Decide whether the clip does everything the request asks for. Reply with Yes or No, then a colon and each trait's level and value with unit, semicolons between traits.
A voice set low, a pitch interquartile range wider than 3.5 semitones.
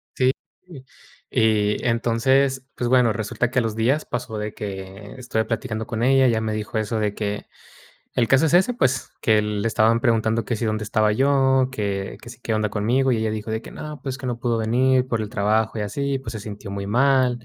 No: low, 115 Hz; average, 3.2 semitones